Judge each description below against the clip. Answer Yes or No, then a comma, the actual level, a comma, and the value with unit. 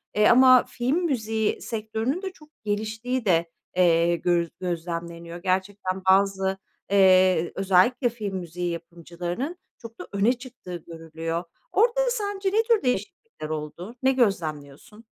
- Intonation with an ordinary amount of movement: No, wide, 6.1 semitones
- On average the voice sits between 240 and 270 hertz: No, high, 195 Hz